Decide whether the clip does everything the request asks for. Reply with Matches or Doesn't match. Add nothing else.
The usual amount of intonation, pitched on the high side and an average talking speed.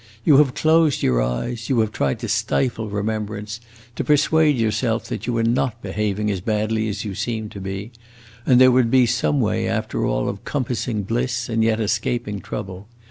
Doesn't match